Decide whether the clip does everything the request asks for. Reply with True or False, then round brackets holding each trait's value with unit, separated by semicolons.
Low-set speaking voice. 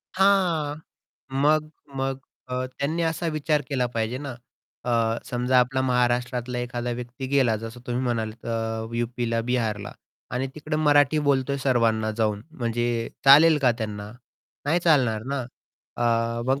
True (125 Hz)